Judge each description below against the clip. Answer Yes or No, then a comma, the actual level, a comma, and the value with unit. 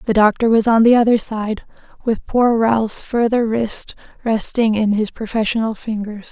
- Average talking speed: Yes, average, 160 wpm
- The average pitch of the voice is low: No, high, 220 Hz